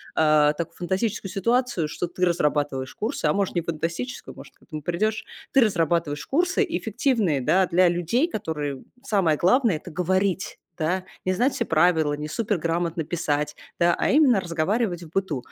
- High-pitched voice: No, medium, 175 Hz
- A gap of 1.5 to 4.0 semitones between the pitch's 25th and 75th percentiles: No, average, 5.0 semitones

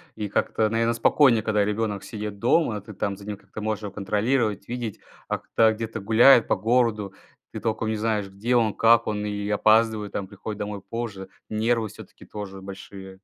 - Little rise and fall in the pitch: Yes, narrow, 1.9 semitones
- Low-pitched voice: Yes, low, 110 Hz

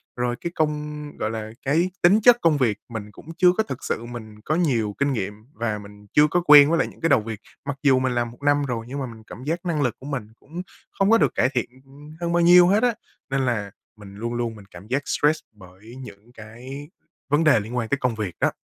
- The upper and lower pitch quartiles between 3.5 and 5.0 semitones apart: No, wide, 5.4 semitones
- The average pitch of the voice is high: No, low, 130 Hz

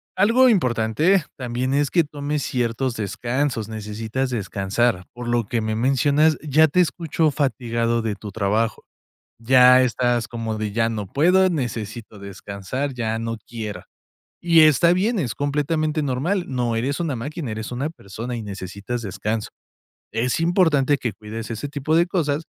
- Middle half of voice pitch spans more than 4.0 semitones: Yes, average, 5.0 semitones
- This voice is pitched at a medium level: No, low, 125 Hz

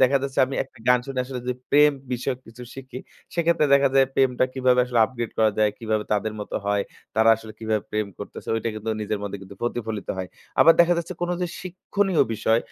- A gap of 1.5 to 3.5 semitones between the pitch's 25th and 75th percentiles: No, average, 4.0 semitones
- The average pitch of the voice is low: Yes, low, 125 Hz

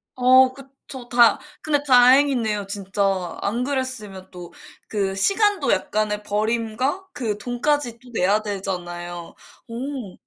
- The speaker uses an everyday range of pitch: Yes, average, 4.8 semitones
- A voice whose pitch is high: Yes, high, 230 Hz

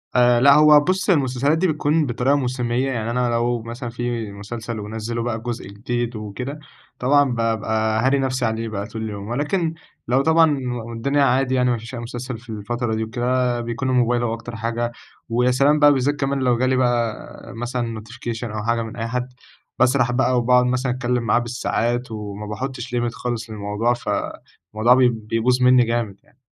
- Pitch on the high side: No, low, 120 Hz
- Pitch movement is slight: Yes, narrow, 2.1 semitones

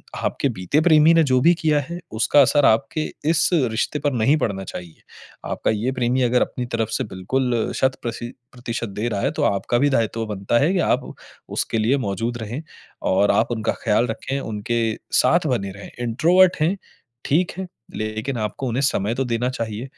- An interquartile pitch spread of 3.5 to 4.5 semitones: Yes, average, 4.1 semitones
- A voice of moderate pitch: No, low, 120 Hz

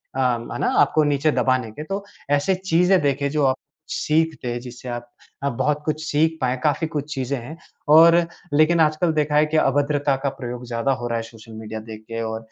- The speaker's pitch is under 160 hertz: Yes, medium, 140 Hz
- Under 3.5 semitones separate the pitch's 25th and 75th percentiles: No, average, 4.2 semitones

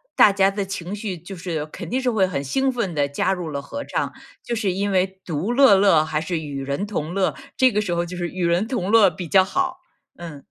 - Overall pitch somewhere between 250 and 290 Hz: No, medium, 185 Hz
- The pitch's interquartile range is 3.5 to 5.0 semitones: Yes, average, 3.8 semitones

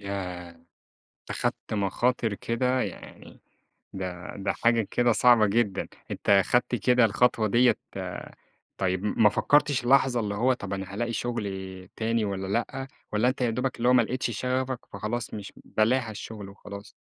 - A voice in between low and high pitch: No, low, 115 Hz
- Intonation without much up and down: No, average, 3.7 semitones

